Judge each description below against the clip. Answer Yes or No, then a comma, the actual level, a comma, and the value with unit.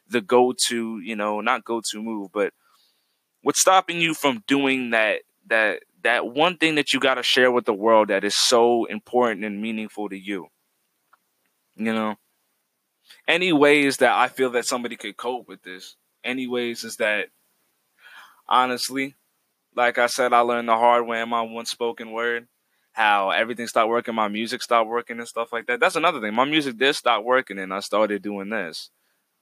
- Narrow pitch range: Yes, narrow, 2.2 semitones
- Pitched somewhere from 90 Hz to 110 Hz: No, low, 120 Hz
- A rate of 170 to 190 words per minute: Yes, average, 180 wpm